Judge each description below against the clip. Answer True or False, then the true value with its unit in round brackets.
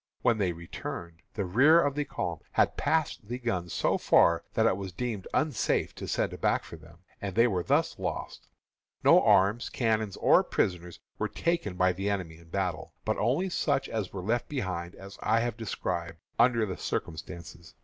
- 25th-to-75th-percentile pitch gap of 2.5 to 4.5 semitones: False (5.2 semitones)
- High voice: False (100 Hz)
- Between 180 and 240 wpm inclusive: True (185 wpm)